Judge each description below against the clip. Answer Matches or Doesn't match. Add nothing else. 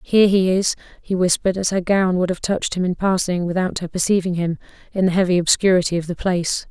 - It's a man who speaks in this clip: Doesn't match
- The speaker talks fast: Matches